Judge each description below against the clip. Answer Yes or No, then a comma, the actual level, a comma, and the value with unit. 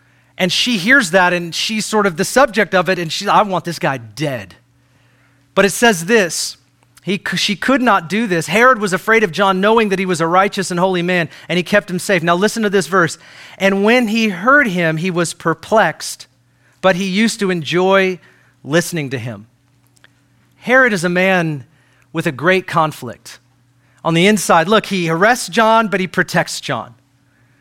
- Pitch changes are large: Yes, wide, 6.8 semitones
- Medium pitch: Yes, medium, 180 Hz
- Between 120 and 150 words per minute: No, average, 190 wpm